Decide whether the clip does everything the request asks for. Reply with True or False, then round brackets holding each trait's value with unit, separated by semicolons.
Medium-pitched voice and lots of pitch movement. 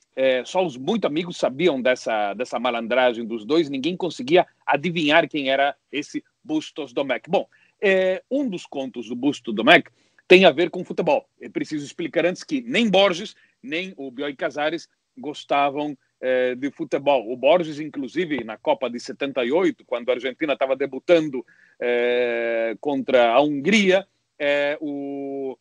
True (150 Hz; 6.0 semitones)